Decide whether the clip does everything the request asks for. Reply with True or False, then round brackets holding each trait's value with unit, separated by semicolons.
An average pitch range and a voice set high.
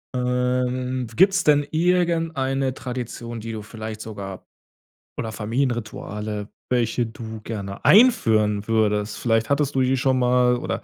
False (3.3 semitones; 125 Hz)